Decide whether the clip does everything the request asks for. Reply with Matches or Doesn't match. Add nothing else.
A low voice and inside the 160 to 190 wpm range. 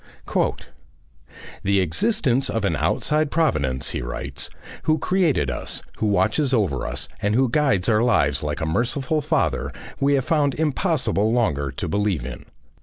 Doesn't match